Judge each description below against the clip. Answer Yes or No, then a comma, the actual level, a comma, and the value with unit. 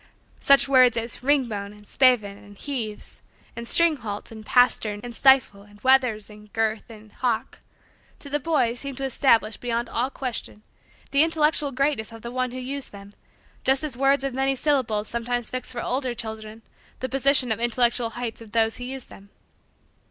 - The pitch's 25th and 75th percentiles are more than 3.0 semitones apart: Yes, average, 3.4 semitones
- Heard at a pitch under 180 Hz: No, high, 245 Hz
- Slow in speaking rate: No, average, 180 wpm